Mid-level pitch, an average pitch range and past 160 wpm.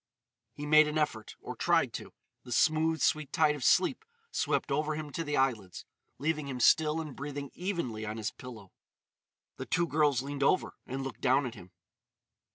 Yes: medium, 145 Hz; average, 3.4 semitones; average, 175 wpm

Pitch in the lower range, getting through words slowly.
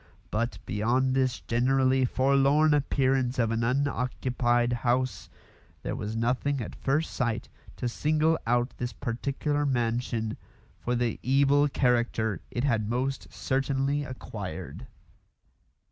Yes: low, 125 Hz; slow, 115 wpm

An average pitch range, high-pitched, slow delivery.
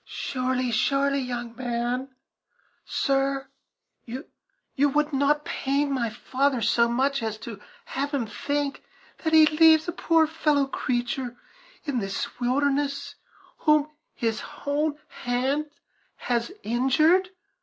Yes: average, 3.2 semitones; very high, 275 Hz; slow, 110 wpm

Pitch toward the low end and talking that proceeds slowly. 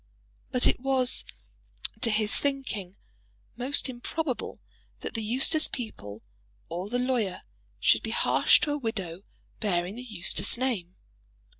No: high, 230 Hz; slow, 130 wpm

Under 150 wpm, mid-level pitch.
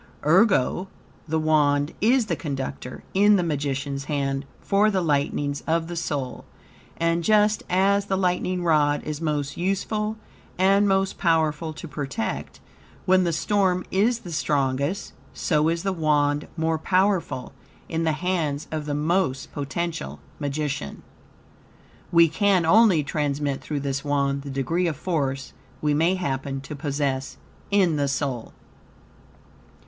Yes: average, 140 wpm; medium, 155 Hz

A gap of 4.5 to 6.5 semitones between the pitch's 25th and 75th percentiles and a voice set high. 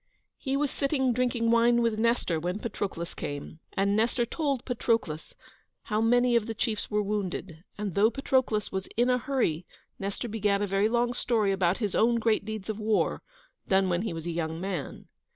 No: average, 3.7 semitones; high, 215 Hz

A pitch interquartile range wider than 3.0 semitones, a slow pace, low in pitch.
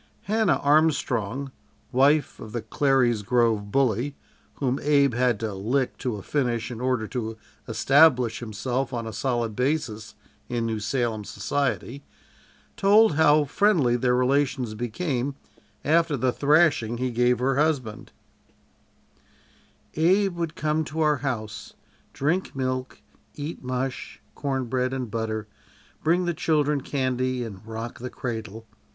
Yes: average, 3.9 semitones; slow, 130 wpm; low, 130 Hz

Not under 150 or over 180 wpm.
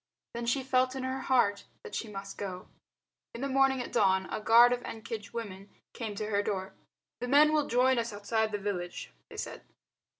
No: average, 200 wpm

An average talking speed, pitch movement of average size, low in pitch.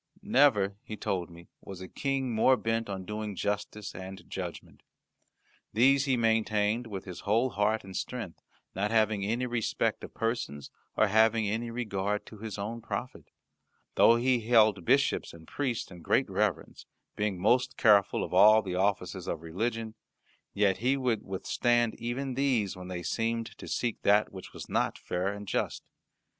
Yes: average, 165 wpm; average, 3.2 semitones; low, 110 Hz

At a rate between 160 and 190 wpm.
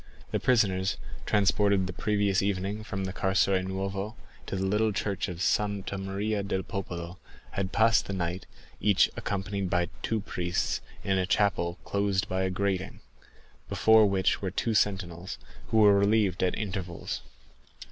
No: average, 150 wpm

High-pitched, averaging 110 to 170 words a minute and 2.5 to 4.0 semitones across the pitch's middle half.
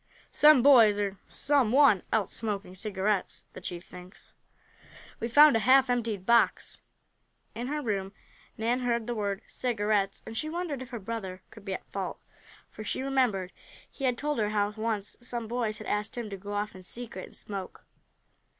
No: high, 220 Hz; average, 180 wpm; average, 3.6 semitones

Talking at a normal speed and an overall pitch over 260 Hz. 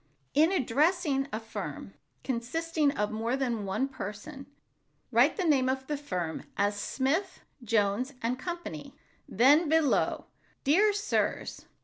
No: slow, 125 wpm; very high, 270 Hz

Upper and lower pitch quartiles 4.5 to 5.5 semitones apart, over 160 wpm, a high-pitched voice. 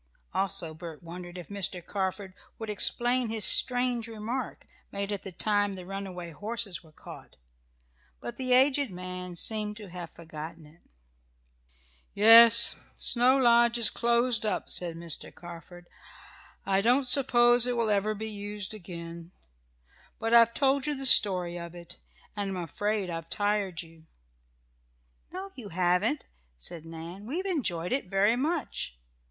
No: average, 5.1 semitones; average, 145 wpm; high, 205 Hz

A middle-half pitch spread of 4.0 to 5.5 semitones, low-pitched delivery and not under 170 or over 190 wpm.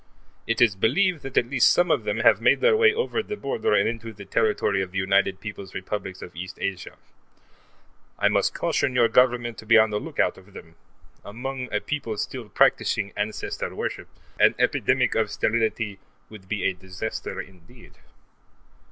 Yes: average, 4.4 semitones; low, 110 Hz; average, 180 wpm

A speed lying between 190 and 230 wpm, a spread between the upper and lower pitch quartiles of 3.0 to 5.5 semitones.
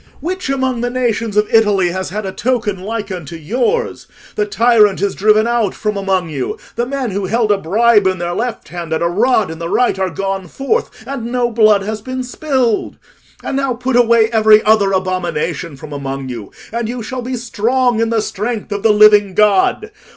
Yes: average, 200 wpm; average, 4.2 semitones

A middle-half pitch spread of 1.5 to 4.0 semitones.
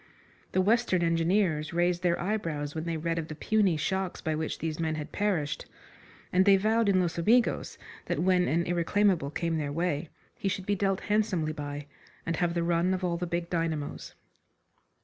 Yes: average, 2.9 semitones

